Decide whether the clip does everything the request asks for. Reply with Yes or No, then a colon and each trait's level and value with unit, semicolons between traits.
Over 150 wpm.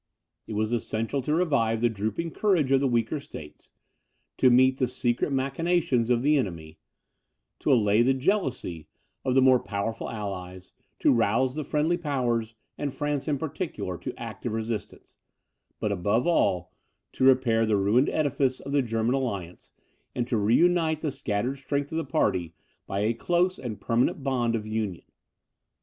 Yes: average, 165 wpm